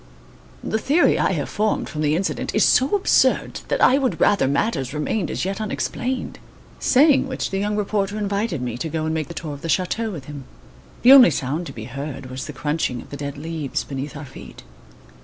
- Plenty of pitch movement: Yes, wide, 6.9 semitones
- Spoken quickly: Yes, fast, 215 wpm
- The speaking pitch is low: No, medium, 160 Hz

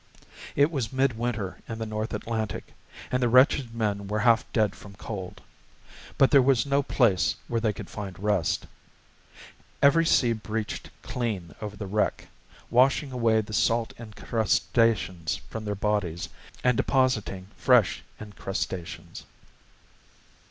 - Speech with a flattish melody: No, average, 3.3 semitones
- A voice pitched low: Yes, low, 110 Hz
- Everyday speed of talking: No, slow, 130 wpm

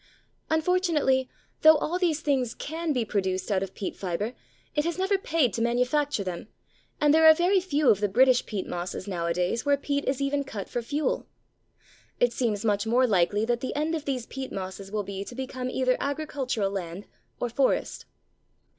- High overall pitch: Yes, very high, 255 Hz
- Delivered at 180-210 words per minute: Yes, average, 185 wpm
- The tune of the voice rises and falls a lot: Yes, wide, 6.4 semitones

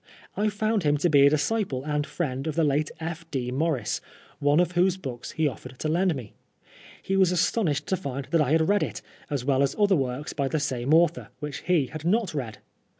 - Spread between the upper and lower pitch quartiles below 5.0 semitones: Yes, average, 4.1 semitones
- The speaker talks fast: Yes, fast, 220 wpm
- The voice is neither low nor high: Yes, medium, 155 Hz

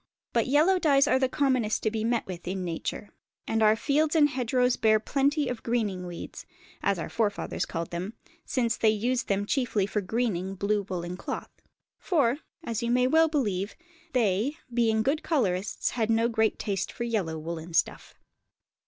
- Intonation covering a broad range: No, average, 4.6 semitones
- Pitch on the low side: No, high, 225 Hz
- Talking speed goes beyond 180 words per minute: No, average, 175 wpm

